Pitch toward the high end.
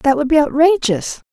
Yes: very high, 285 Hz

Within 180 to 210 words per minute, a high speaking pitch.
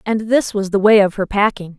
No: fast, 270 wpm; high, 205 Hz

